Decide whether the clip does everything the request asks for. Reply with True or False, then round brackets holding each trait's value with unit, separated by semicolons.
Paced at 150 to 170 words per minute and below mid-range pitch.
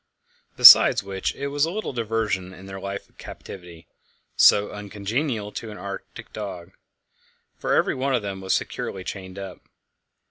True (155 wpm; 100 Hz)